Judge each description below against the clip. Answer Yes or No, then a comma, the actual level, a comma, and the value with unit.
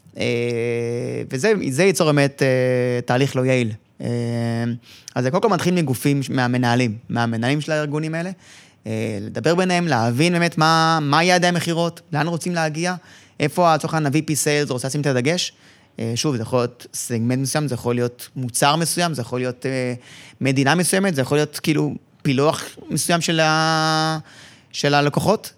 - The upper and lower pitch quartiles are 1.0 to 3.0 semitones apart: No, average, 4.7 semitones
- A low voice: No, medium, 145 Hz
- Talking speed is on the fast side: Yes, fast, 155 wpm